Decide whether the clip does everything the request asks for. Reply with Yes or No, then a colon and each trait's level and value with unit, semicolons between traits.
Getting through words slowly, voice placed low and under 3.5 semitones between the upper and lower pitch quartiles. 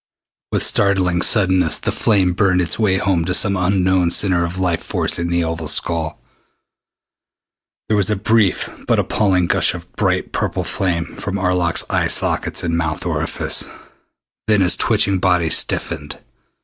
No: average, 155 wpm; very low, 90 Hz; narrow, 2.4 semitones